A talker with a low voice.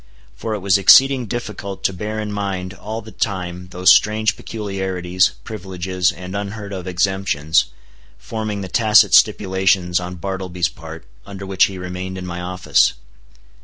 Yes: very low, 95 Hz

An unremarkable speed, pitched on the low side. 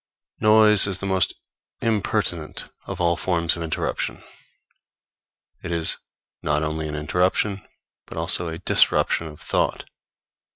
No: slow, 125 wpm; very low, 85 Hz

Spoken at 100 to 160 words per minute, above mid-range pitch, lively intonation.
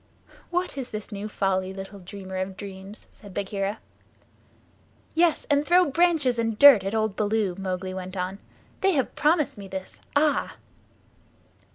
Yes: average, 150 wpm; high, 205 Hz; wide, 6.8 semitones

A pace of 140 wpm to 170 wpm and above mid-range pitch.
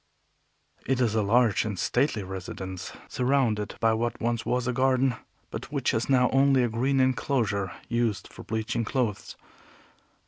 No: average, 150 wpm; low, 120 Hz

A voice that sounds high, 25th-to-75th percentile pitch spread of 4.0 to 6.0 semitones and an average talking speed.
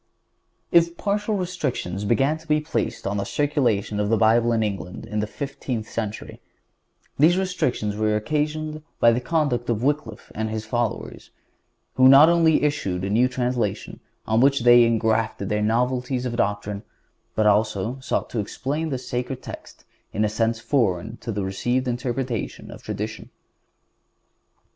No: low, 120 Hz; average, 4.7 semitones; average, 160 wpm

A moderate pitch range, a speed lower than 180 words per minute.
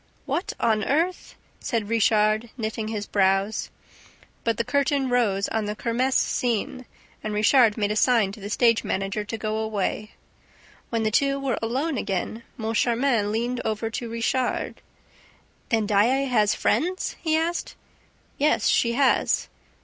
Yes: average, 3.2 semitones; average, 150 wpm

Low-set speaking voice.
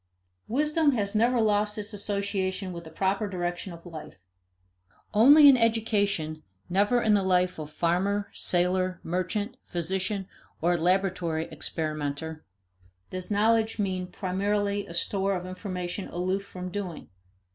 No: high, 190 Hz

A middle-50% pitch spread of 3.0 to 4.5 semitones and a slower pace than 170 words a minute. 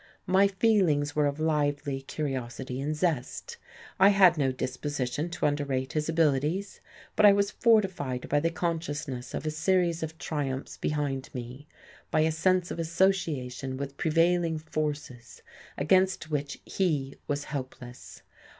Yes: average, 3.9 semitones; average, 140 wpm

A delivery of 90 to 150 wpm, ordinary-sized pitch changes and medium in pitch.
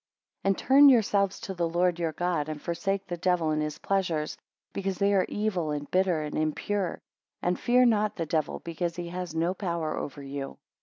No: average, 200 wpm; average, 3.7 semitones; medium, 175 Hz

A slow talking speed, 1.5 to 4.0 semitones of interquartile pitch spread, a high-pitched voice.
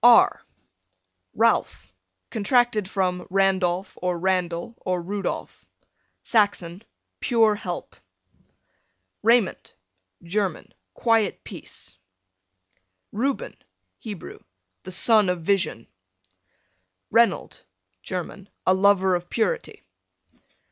Yes: slow, 80 wpm; average, 3.4 semitones; high, 195 Hz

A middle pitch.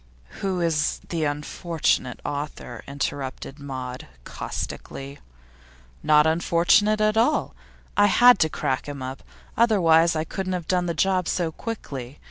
Yes: medium, 160 Hz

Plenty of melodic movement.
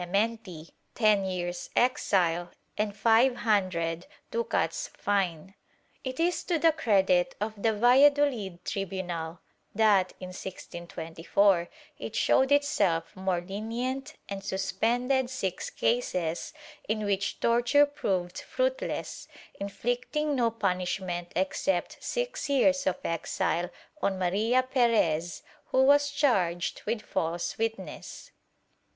Yes: wide, 5.9 semitones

